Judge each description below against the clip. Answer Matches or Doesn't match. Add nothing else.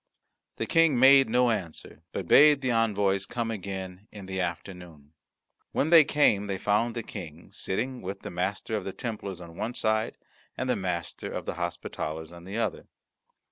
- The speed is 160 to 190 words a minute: Matches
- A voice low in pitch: Matches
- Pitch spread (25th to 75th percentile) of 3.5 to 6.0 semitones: Matches